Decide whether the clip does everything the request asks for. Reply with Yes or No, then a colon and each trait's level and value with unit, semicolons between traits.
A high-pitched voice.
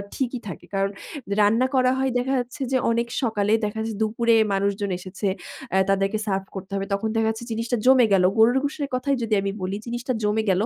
Yes: high, 220 Hz